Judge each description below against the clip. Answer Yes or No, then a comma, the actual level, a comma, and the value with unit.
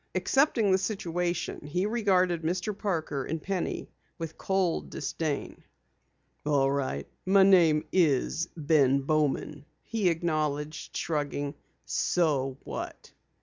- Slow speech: Yes, slow, 105 wpm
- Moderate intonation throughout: Yes, average, 4.1 semitones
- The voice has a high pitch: No, medium, 165 Hz